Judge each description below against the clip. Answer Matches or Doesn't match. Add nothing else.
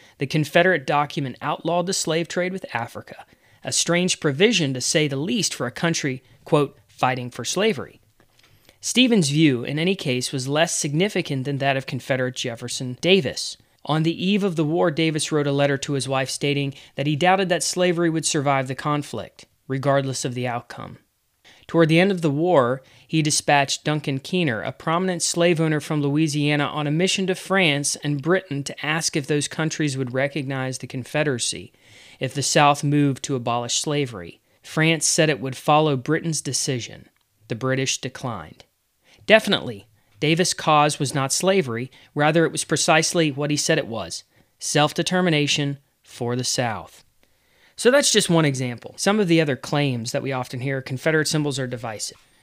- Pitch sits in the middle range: Matches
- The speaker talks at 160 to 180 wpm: Matches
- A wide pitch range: Doesn't match